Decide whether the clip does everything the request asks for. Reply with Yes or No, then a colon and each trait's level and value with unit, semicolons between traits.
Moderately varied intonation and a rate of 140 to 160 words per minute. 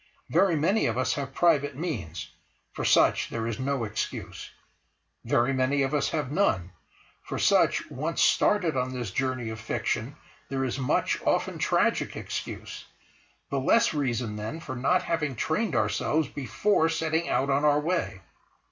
Yes: average, 4.9 semitones; average, 155 wpm